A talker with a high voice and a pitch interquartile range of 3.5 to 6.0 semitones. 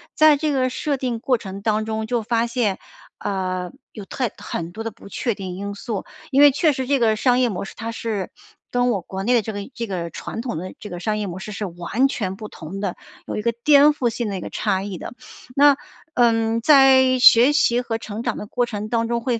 Yes: high, 225 Hz; average, 3.8 semitones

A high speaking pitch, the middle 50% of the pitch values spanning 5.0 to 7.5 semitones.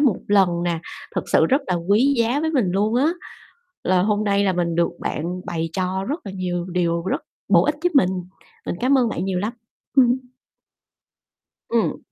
Yes: high, 195 Hz; average, 5.3 semitones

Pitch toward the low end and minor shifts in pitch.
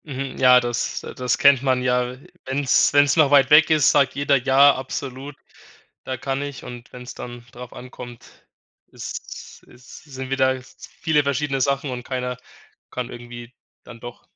Yes: low, 130 Hz; narrow, 2.0 semitones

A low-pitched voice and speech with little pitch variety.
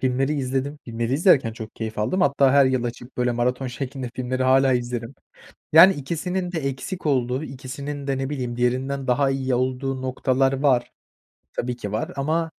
Yes: low, 130 Hz; narrow, 2.0 semitones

